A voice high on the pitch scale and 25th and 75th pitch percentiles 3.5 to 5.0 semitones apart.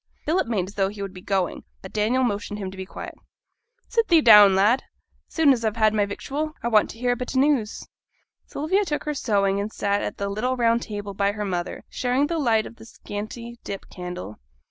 Yes: high, 215 Hz; average, 4.2 semitones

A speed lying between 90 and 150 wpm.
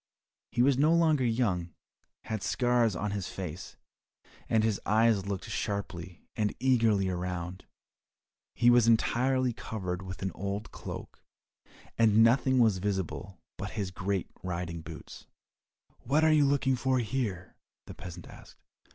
Yes: average, 140 wpm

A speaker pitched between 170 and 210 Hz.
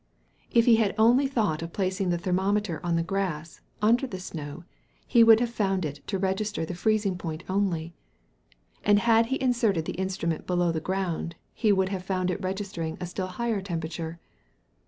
Yes: high, 190 Hz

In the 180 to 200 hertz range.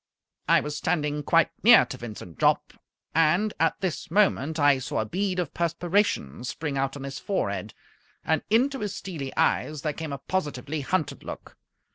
No: medium, 155 Hz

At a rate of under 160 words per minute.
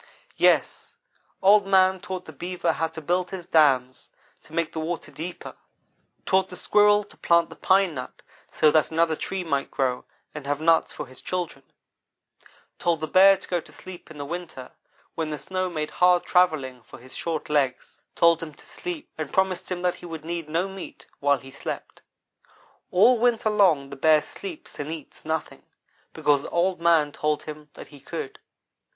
No: average, 185 wpm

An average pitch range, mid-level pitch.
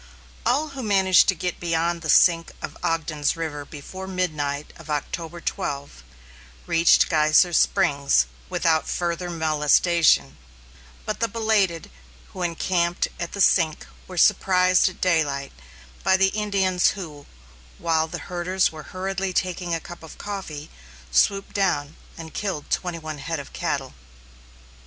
Yes: average, 3.3 semitones; medium, 170 Hz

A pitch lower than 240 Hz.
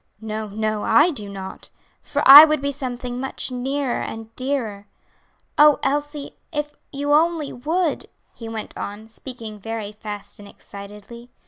No: high, 245 Hz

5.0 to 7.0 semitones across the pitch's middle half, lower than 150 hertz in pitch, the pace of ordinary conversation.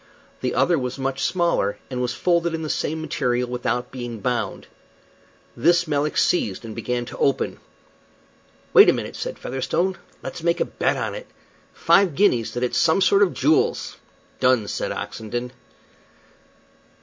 Yes: wide, 5.6 semitones; low, 135 Hz; average, 155 wpm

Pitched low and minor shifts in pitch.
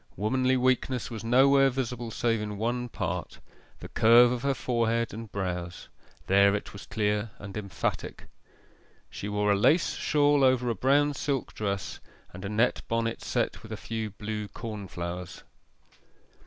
No: low, 115 Hz; average, 3.4 semitones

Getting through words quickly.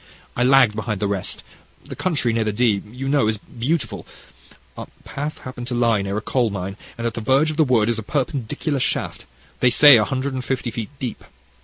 Yes: fast, 215 wpm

